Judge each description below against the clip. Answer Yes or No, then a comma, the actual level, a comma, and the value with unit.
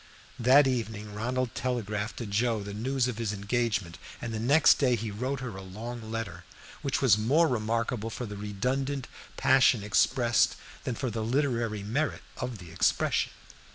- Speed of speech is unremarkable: Yes, average, 165 wpm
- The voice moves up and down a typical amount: Yes, average, 3.3 semitones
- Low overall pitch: Yes, low, 115 Hz